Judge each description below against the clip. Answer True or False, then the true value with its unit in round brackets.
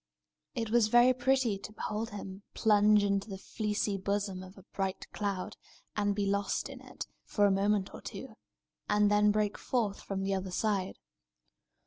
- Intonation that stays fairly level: True (1.4 semitones)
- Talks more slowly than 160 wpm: False (170 wpm)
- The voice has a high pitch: True (205 Hz)